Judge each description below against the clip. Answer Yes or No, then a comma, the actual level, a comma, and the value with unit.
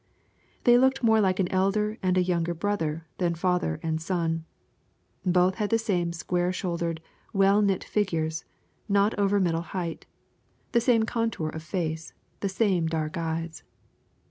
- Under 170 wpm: Yes, average, 150 wpm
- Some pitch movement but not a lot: Yes, average, 3.7 semitones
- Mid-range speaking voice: Yes, medium, 180 Hz